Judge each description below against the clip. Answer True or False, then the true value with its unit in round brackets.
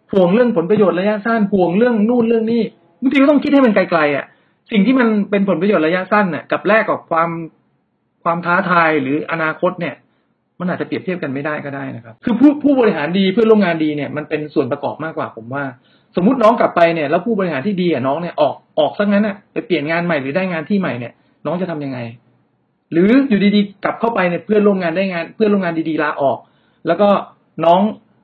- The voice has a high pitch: False (180 Hz)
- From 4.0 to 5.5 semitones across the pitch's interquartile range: True (5.1 semitones)